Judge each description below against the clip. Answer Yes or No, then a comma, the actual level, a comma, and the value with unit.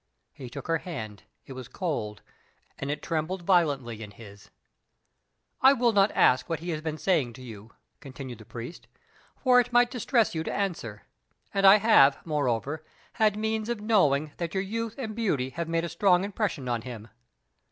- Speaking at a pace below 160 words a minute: No, average, 185 wpm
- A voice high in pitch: No, medium, 165 Hz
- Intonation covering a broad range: Yes, wide, 8.2 semitones